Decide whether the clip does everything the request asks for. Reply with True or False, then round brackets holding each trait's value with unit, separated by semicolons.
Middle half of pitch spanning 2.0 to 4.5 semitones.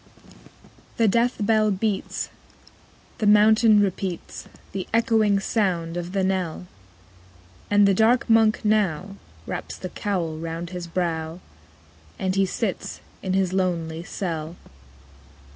True (3.6 semitones)